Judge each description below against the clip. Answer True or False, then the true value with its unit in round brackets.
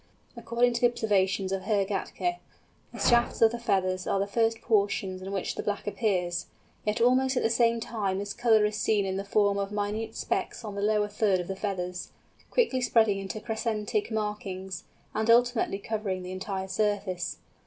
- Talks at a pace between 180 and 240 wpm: True (185 wpm)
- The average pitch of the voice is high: True (210 Hz)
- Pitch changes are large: False (2.8 semitones)